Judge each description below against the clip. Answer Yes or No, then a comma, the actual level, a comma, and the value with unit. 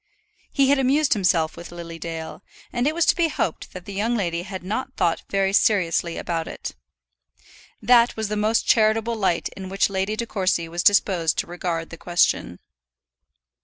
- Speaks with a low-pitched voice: No, high, 195 Hz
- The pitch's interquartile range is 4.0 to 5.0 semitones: Yes, average, 4.6 semitones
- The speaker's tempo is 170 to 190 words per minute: Yes, average, 180 wpm